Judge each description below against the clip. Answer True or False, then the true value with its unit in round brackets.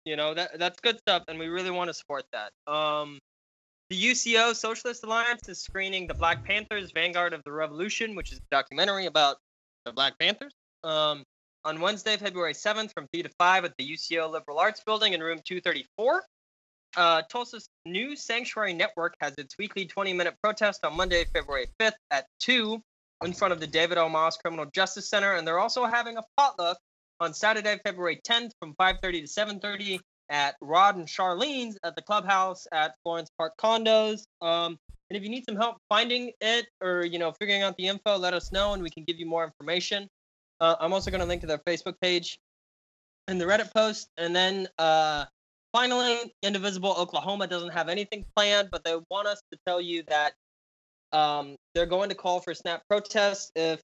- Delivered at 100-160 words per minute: False (195 wpm)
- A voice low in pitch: False (185 Hz)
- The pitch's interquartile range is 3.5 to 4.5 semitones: True (4.2 semitones)